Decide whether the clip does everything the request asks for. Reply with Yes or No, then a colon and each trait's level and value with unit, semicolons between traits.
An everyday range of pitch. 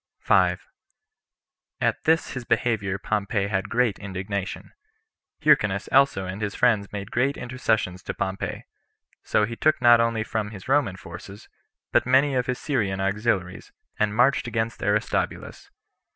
Yes: average, 3.8 semitones